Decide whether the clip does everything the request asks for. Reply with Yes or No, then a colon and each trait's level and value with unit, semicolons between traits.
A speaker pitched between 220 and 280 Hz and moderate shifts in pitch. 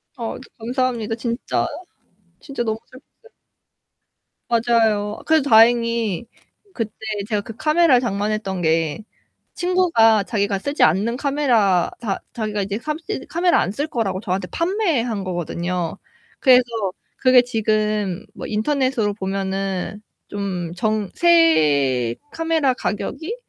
Yes: high, 225 Hz; average, 4.8 semitones